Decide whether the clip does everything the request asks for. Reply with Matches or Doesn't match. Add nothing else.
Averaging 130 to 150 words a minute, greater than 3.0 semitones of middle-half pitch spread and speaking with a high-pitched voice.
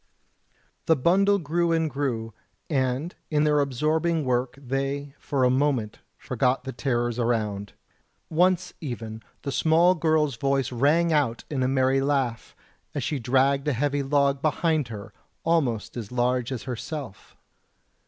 Doesn't match